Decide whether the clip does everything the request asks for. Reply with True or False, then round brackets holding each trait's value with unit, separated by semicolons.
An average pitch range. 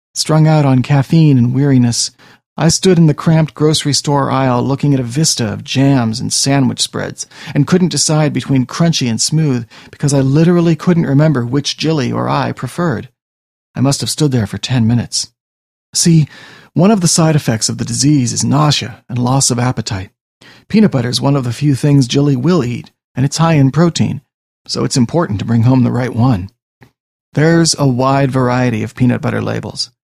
True (4.0 semitones)